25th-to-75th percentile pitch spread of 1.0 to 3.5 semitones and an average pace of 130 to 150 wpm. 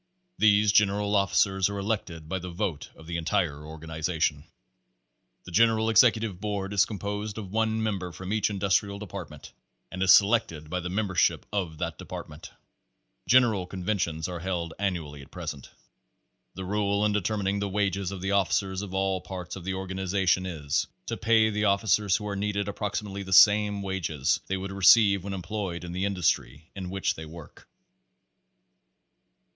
No: narrow, 2.5 semitones; average, 165 wpm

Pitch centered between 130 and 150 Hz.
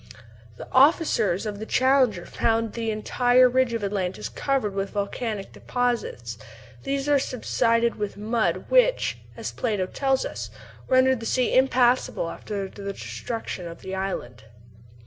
No: high, 230 Hz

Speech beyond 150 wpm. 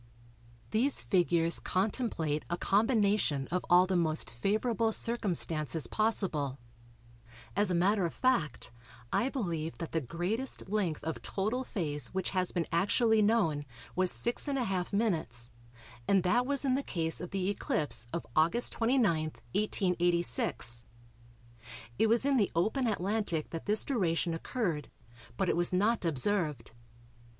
No: slow, 135 wpm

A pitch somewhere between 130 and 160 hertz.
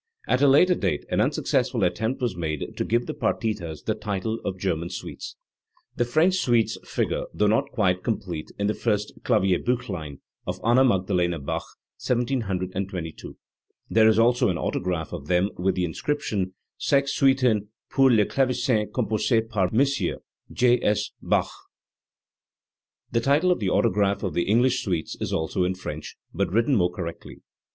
No: low, 105 Hz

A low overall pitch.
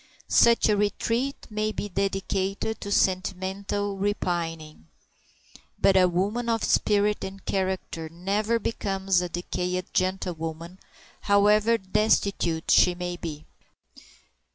No: high, 195 Hz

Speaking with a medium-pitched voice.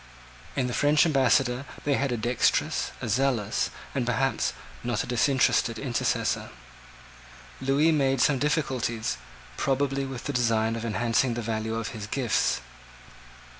No: low, 125 Hz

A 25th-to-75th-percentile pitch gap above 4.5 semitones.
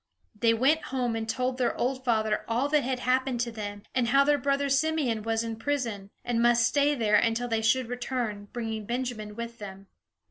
No: average, 2.7 semitones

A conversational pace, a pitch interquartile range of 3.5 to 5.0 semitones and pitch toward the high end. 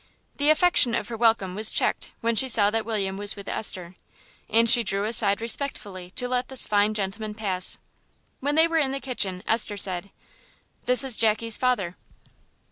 Yes: average, 180 wpm; average, 3.8 semitones; high, 220 Hz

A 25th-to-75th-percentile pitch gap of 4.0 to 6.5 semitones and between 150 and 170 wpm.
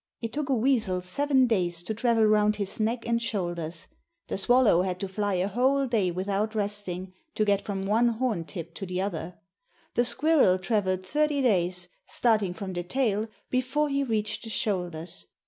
No: average, 4.5 semitones; average, 180 wpm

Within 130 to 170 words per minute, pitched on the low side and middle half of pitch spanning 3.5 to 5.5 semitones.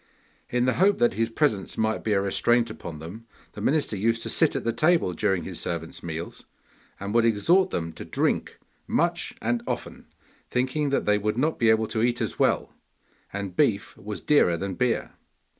No: average, 190 wpm; low, 110 Hz; average, 3.8 semitones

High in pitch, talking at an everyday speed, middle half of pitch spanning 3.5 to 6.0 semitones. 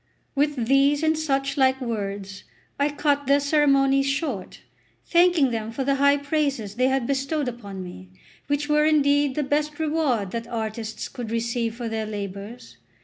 Yes: very high, 270 Hz; average, 160 wpm; average, 4.2 semitones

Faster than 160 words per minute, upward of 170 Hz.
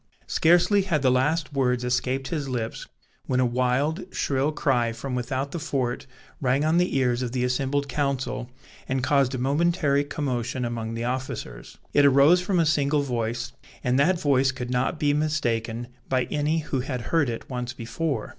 No: average, 175 wpm; low, 135 Hz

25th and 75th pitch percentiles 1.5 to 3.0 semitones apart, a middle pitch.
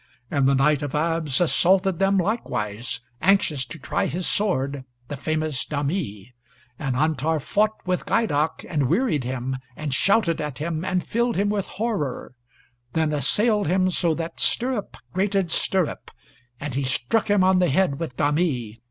No: wide, 5.6 semitones; medium, 160 Hz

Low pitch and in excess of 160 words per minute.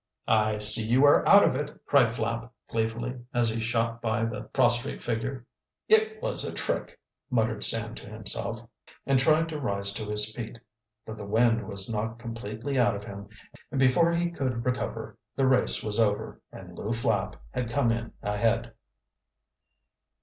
Yes: low, 115 Hz; average, 170 wpm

